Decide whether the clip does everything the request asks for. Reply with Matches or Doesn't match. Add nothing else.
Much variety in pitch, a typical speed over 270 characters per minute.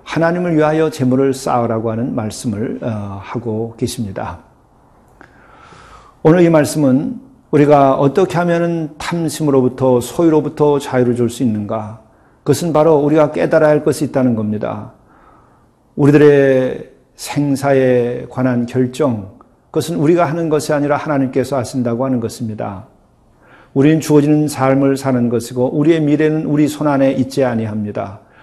Doesn't match